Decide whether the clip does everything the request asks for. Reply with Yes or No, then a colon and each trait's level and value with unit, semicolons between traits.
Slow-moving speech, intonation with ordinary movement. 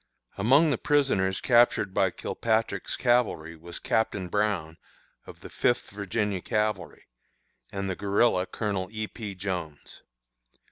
Yes: slow, 125 wpm; average, 3.2 semitones